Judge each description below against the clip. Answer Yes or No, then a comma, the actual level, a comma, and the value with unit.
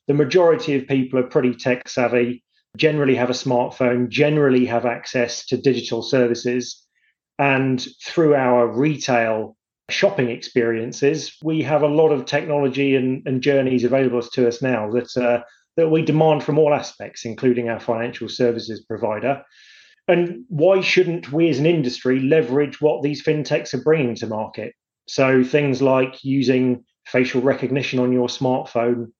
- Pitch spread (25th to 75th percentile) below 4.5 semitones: Yes, average, 3.4 semitones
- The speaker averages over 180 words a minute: No, average, 150 wpm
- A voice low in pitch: Yes, low, 130 Hz